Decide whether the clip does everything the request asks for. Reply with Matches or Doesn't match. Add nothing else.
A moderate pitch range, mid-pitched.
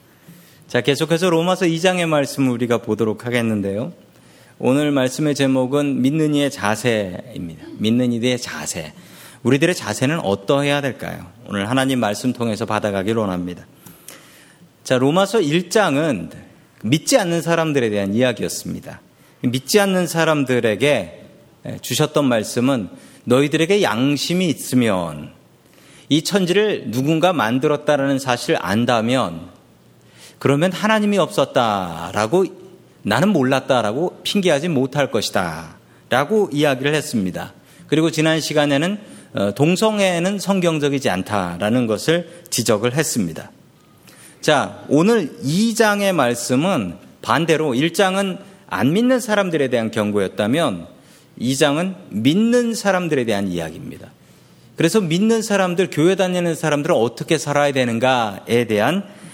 Doesn't match